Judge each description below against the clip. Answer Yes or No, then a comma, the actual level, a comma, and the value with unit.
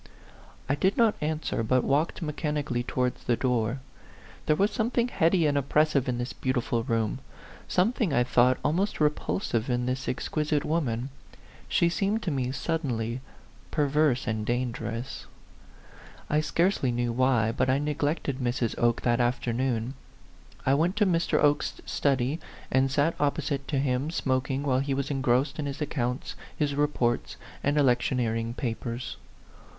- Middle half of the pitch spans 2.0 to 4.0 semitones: Yes, average, 3.6 semitones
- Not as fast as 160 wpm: Yes, average, 150 wpm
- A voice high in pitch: No, low, 135 Hz